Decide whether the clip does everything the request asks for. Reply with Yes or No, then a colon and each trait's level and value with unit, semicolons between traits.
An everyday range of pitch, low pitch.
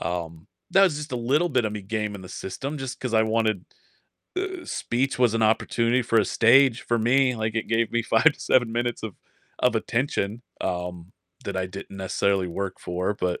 Yes: average, 4.2 semitones; low, 115 Hz